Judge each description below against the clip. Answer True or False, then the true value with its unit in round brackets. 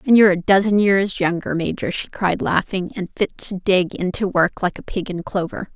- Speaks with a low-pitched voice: False (190 Hz)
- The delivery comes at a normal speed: False (220 wpm)